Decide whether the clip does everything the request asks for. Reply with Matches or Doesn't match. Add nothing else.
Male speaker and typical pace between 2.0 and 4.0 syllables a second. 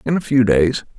Doesn't match